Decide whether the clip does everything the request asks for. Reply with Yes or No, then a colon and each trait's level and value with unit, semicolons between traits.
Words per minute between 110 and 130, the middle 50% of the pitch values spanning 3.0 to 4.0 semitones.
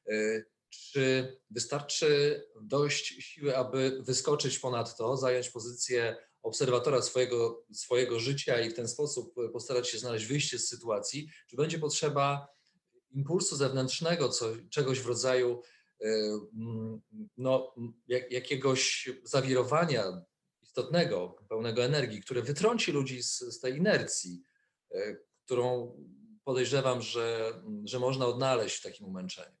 Yes: average, 115 wpm; average, 3.3 semitones